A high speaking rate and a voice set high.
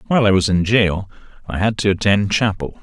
No: fast, 210 wpm; low, 100 Hz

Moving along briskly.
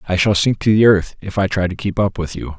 Yes: fast, 325 wpm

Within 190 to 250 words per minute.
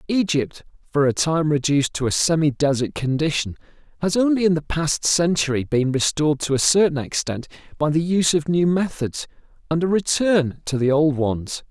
No: average, 180 wpm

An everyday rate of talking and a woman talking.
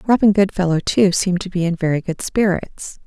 Yes: average, 195 wpm; female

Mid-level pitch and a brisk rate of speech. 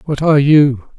No: medium, 150 Hz; average, 185 wpm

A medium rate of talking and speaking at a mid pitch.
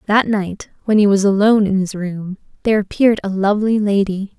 No: average, 190 wpm; high, 200 Hz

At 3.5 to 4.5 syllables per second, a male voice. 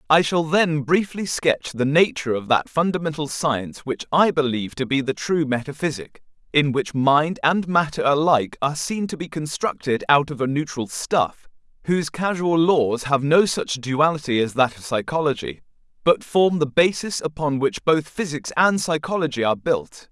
No: 5.0 syllables/s; male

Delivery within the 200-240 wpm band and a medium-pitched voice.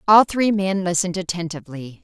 No: average, 150 wpm; medium, 180 Hz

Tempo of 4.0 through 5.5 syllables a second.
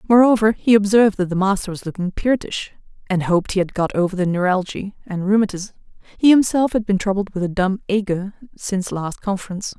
No: 6.1 syllables/s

